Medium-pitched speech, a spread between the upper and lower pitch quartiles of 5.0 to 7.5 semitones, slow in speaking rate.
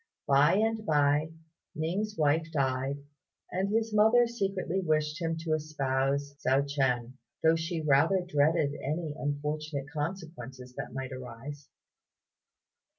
No: medium, 150 Hz; average, 3.6 semitones; slow, 120 wpm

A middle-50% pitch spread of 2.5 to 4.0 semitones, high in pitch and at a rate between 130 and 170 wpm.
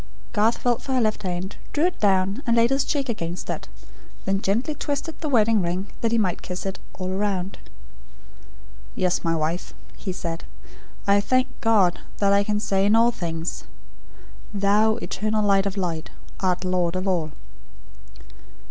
Yes: average, 3.6 semitones; high, 200 Hz; average, 165 wpm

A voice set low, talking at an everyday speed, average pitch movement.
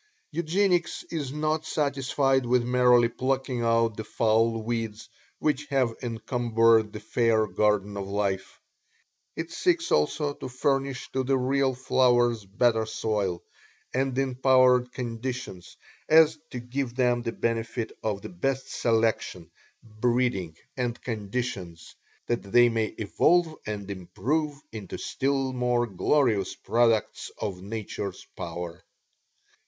No: low, 120 Hz; slow, 120 wpm; average, 3.5 semitones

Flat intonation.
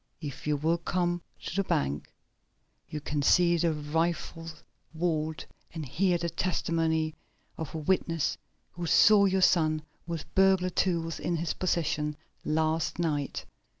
Yes: narrow, 2.1 semitones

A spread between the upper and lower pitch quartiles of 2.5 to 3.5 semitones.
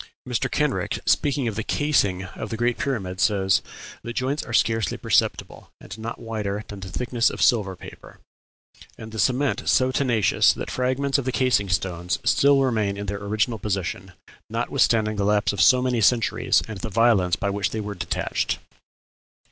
No: average, 4.0 semitones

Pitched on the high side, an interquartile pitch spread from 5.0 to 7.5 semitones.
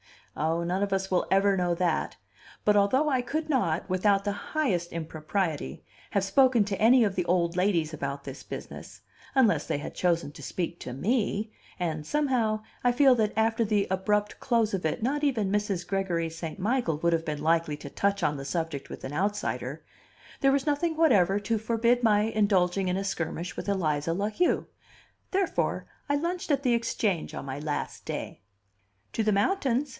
Yes: high, 200 Hz; wide, 5.6 semitones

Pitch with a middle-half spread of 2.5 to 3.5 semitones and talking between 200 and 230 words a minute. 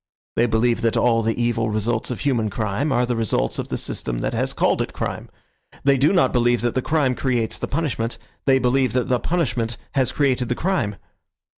Yes: average, 2.8 semitones; fast, 205 wpm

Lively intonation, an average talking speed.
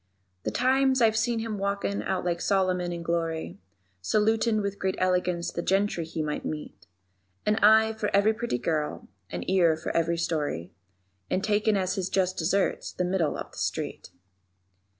No: average, 4.0 semitones; average, 170 wpm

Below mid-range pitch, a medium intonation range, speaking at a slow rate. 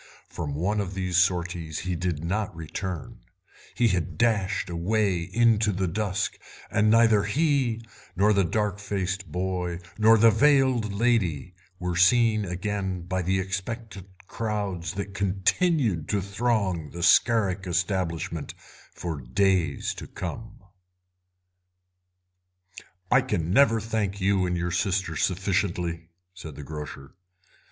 Yes: very low, 95 Hz; average, 3.4 semitones; slow, 125 wpm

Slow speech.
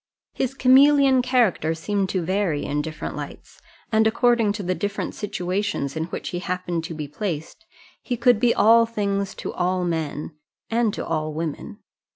No: average, 170 wpm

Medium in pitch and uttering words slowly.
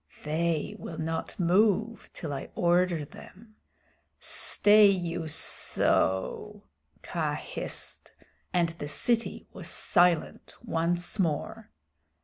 Yes: medium, 175 Hz; slow, 100 wpm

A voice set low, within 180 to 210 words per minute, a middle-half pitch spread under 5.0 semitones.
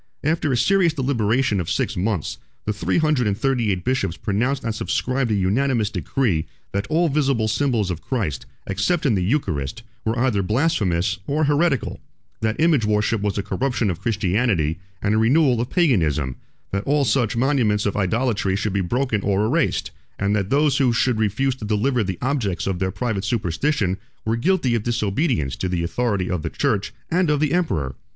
No: low, 110 Hz; average, 185 wpm; wide, 5.6 semitones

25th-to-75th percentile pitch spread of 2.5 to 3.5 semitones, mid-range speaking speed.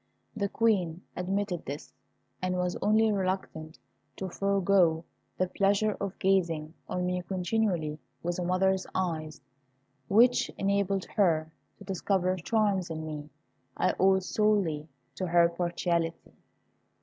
No: average, 2.8 semitones; slow, 125 wpm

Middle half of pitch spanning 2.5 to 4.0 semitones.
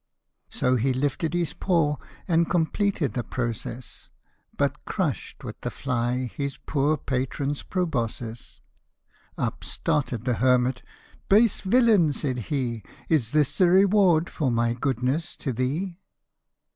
No: average, 5.2 semitones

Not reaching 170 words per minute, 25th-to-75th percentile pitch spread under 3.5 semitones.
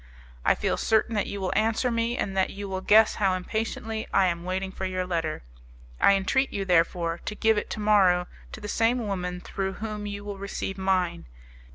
No: fast, 205 wpm; average, 2.7 semitones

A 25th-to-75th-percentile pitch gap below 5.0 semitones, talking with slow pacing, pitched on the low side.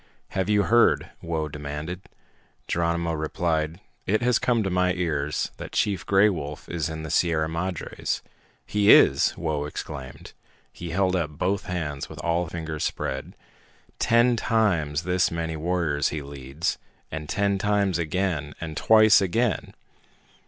No: average, 3.9 semitones; average, 145 wpm; very low, 85 Hz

